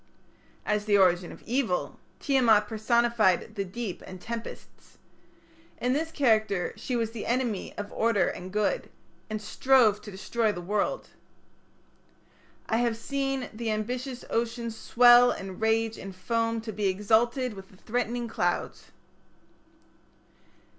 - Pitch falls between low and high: No, high, 225 Hz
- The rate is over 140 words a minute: No, slow, 135 wpm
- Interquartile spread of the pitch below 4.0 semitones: Yes, average, 2.7 semitones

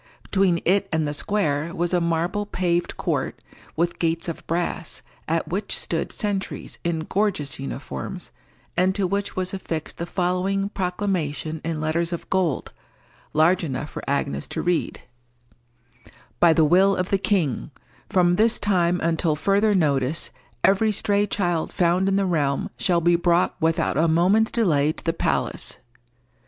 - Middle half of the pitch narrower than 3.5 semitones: Yes, average, 3.1 semitones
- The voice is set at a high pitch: No, medium, 175 Hz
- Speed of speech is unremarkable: Yes, average, 155 wpm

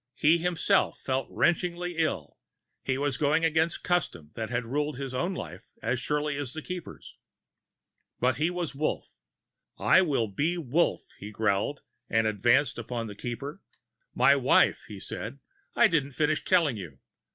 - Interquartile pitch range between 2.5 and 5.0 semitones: No, wide, 5.5 semitones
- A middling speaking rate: Yes, average, 155 wpm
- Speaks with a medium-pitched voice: Yes, medium, 145 Hz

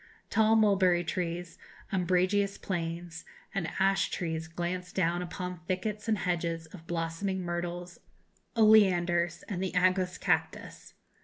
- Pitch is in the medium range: Yes, medium, 180 Hz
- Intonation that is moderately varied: No, narrow, 2.0 semitones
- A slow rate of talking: Yes, slow, 115 wpm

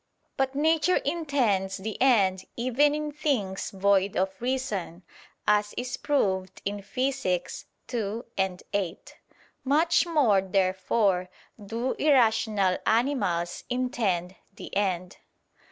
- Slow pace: Yes, slow, 105 wpm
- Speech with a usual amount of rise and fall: No, wide, 5.7 semitones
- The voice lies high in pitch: Yes, high, 210 Hz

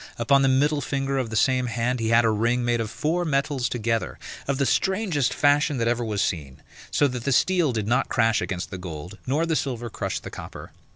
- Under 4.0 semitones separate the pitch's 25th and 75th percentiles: Yes, average, 3.6 semitones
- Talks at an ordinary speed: No, fast, 225 wpm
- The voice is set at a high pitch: No, low, 125 Hz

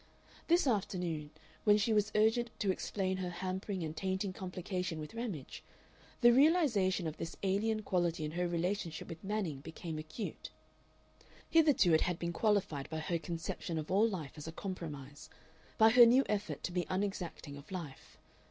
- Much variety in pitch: No, average, 4.4 semitones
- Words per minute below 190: Yes, average, 165 wpm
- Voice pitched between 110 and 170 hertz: No, medium, 185 Hz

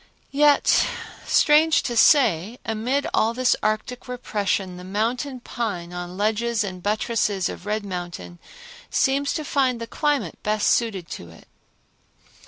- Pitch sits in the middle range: No, high, 220 Hz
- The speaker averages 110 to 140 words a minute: Yes, slow, 135 wpm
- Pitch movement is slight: No, average, 4.8 semitones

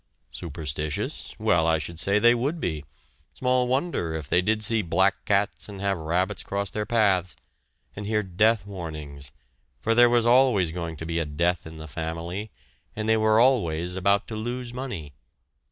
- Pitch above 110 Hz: No, very low, 95 Hz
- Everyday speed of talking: Yes, average, 175 wpm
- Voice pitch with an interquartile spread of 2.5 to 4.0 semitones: No, average, 5.3 semitones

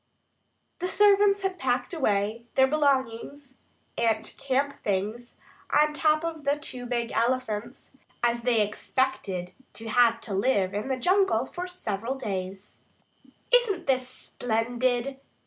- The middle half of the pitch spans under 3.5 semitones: No, average, 4.2 semitones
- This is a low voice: No, very high, 255 Hz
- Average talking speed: No, slow, 130 wpm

